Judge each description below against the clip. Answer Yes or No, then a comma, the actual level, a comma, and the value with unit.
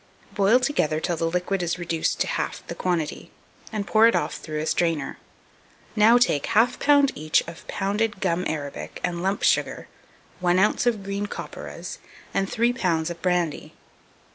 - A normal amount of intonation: Yes, average, 4.4 semitones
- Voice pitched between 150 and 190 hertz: Yes, medium, 185 Hz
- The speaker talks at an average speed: Yes, average, 165 wpm